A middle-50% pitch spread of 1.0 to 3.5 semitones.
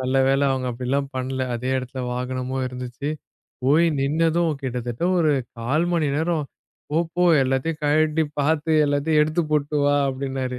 Yes: average, 3.2 semitones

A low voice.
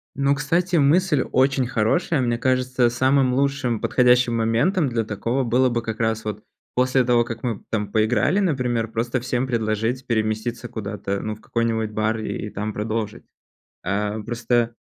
Yes: low, 120 Hz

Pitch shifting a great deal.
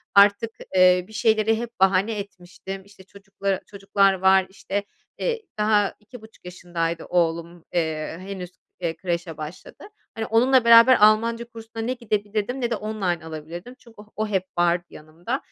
No: average, 3.9 semitones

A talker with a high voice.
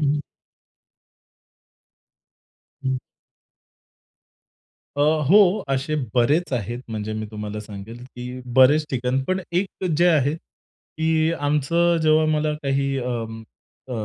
No: medium, 140 Hz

